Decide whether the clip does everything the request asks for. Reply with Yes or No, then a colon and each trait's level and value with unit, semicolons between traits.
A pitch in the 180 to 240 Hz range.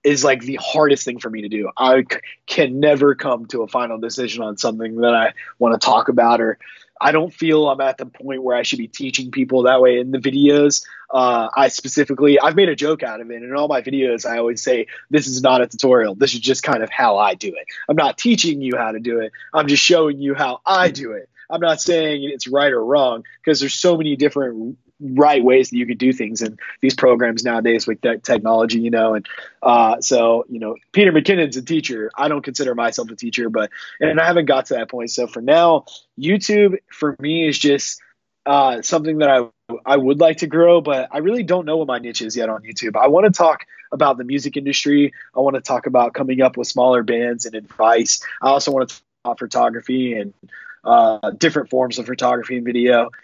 No: low, 130 Hz